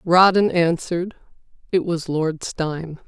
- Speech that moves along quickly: No, slow, 115 wpm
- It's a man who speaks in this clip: No, female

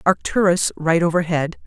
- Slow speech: Yes, slow, 110 wpm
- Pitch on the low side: No, medium, 170 Hz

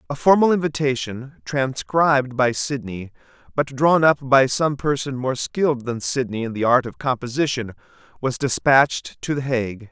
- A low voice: Yes, low, 130 Hz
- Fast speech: No, average, 155 wpm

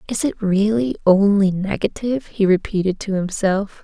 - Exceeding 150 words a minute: No, average, 140 wpm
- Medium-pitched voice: No, high, 200 Hz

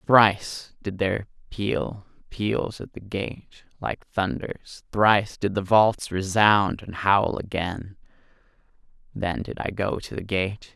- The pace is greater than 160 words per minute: No, average, 140 wpm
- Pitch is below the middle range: Yes, low, 100 Hz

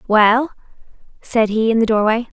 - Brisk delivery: No, average, 150 wpm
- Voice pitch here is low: No, high, 225 Hz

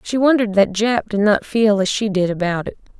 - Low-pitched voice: No, high, 210 Hz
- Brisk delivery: Yes, fast, 240 wpm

